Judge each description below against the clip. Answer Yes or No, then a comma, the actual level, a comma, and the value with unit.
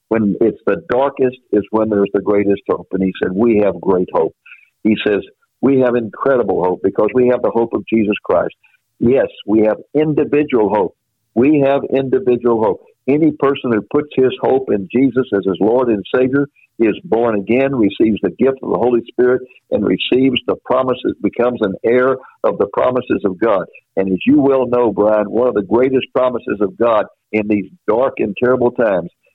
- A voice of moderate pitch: No, low, 125 Hz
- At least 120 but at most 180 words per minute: No, average, 190 wpm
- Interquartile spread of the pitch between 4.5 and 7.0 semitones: No, average, 4.1 semitones